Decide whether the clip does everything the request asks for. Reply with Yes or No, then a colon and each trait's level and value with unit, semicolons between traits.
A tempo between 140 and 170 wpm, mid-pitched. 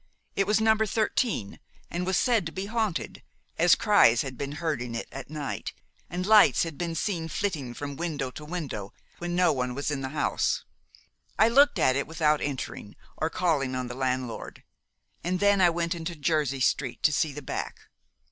No: average, 190 wpm; medium, 160 Hz